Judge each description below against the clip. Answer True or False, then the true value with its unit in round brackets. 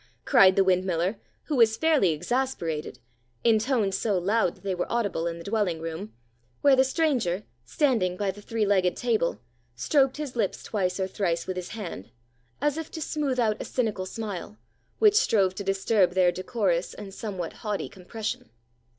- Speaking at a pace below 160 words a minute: False (175 wpm)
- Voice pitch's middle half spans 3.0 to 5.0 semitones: True (4.6 semitones)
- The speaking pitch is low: False (205 Hz)